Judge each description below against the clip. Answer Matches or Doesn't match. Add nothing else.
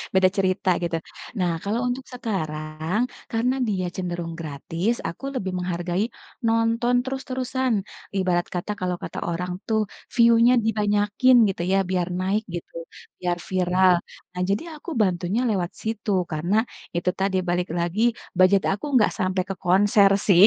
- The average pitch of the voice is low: Doesn't match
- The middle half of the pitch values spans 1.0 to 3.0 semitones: Doesn't match